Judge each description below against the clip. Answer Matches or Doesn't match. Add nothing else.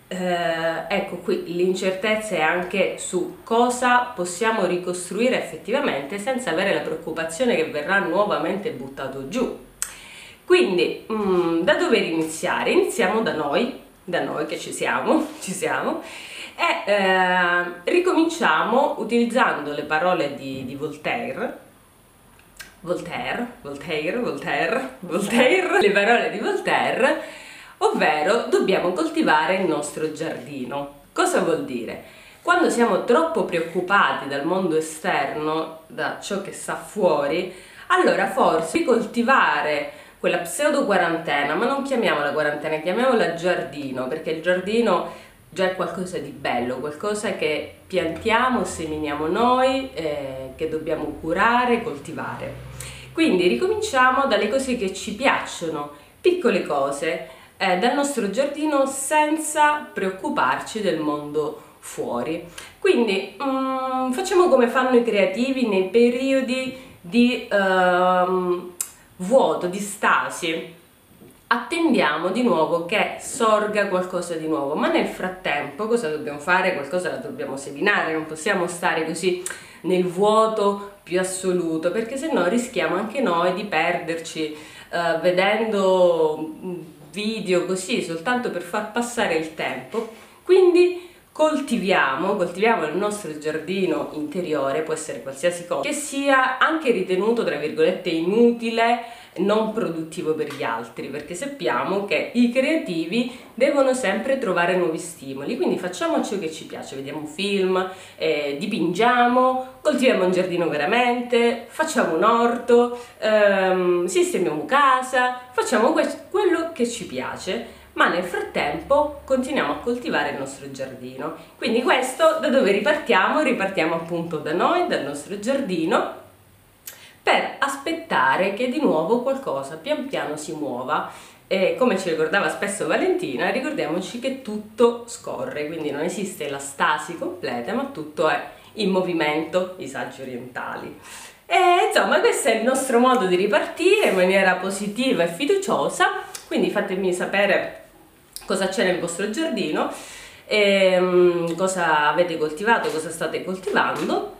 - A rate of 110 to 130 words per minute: Matches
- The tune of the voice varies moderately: Doesn't match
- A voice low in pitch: Doesn't match